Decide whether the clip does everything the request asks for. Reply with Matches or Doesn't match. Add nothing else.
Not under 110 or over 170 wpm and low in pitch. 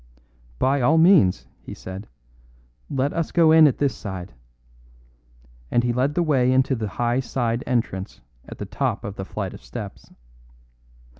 Matches